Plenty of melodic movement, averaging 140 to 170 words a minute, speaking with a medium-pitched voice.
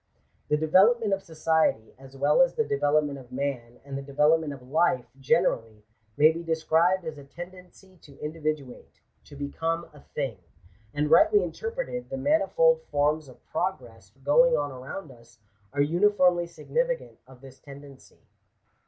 No: average, 4.8 semitones; average, 160 wpm; medium, 150 Hz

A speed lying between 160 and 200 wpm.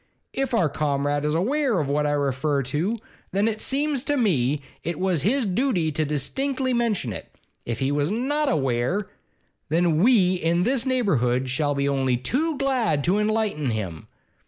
Yes: average, 170 wpm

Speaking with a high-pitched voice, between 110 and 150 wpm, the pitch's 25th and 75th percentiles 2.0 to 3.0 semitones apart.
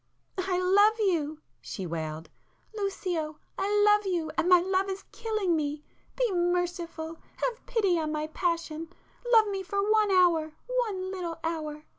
No: very high, 360 Hz; slow, 135 wpm; average, 4.2 semitones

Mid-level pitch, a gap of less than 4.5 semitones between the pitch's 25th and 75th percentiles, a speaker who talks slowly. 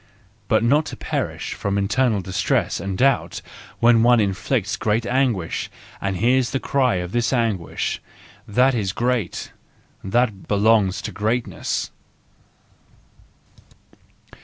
No: low, 115 Hz; average, 3.8 semitones; slow, 110 wpm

